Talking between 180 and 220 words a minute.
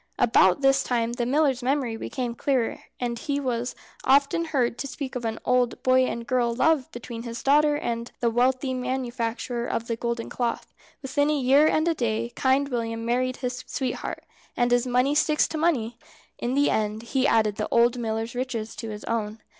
Yes: average, 195 wpm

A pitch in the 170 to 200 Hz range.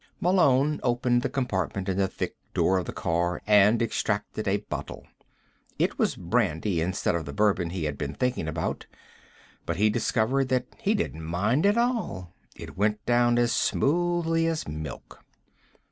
No: low, 110 Hz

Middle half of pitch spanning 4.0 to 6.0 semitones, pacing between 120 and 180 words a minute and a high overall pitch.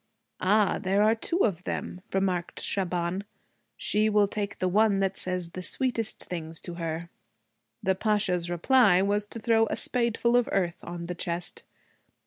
No: average, 3.4 semitones; average, 160 wpm; high, 195 Hz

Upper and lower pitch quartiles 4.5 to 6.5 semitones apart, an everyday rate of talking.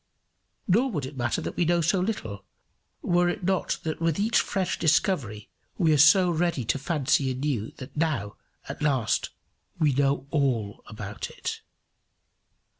Yes: average, 5.3 semitones; average, 155 wpm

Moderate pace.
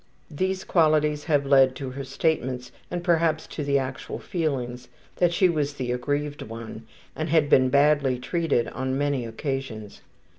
Yes: average, 155 wpm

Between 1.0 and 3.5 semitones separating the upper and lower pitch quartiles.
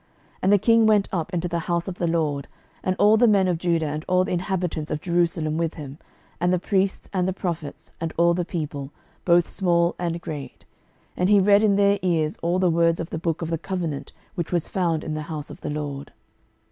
Yes: narrow, 2.6 semitones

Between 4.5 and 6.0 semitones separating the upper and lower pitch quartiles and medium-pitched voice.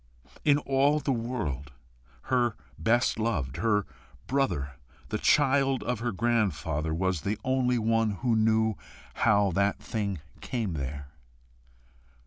No: average, 5.2 semitones; low, 110 Hz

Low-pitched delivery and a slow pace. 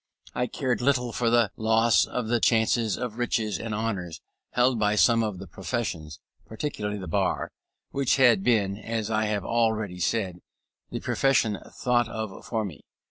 No: low, 110 Hz; average, 170 wpm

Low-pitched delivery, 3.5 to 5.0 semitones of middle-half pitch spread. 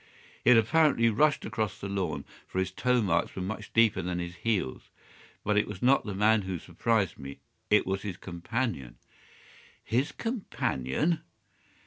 Yes: low, 105 Hz; average, 4.1 semitones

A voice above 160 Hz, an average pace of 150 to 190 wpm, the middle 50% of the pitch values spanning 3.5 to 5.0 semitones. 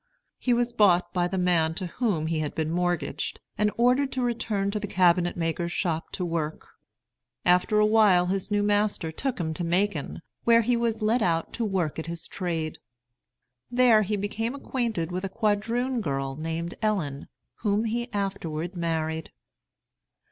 Yes: high, 190 Hz; average, 170 wpm; average, 4.7 semitones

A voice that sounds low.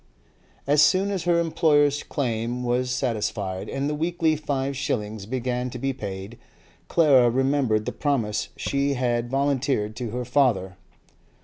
Yes: low, 130 Hz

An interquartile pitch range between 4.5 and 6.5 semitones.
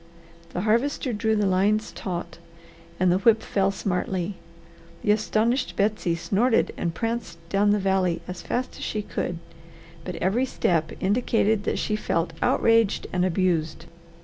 No: average, 3.4 semitones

